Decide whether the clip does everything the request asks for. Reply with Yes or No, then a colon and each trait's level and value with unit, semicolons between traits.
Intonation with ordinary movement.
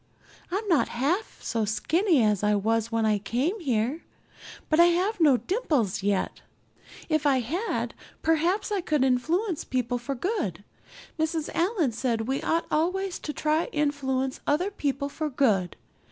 No: wide, 6.3 semitones